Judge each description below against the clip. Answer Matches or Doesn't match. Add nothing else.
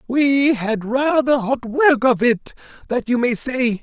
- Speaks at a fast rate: Doesn't match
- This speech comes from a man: Matches